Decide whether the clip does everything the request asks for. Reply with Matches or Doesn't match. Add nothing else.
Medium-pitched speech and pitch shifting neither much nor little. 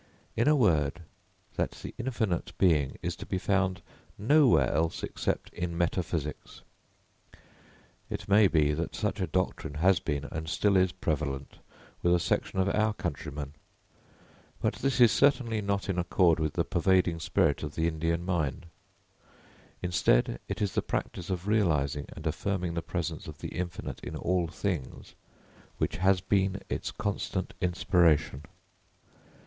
Doesn't match